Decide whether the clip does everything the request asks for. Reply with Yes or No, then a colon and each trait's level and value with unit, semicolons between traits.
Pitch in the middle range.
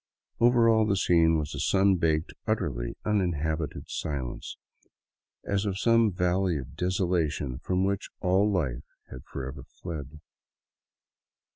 No: very low, 90 Hz